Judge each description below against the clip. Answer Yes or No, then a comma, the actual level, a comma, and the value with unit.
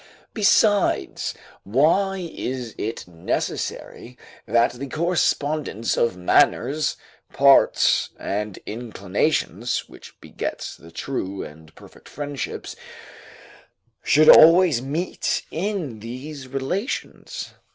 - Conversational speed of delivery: No, slow, 90 wpm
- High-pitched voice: No, low, 135 Hz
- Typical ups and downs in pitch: No, wide, 6.0 semitones